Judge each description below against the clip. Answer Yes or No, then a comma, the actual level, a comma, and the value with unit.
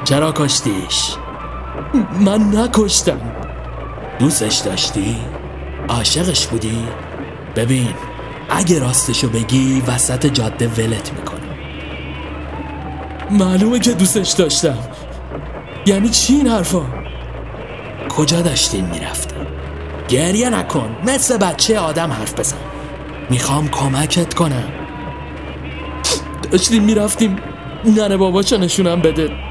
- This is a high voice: No, medium, 140 Hz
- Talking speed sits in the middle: No, slow, 85 wpm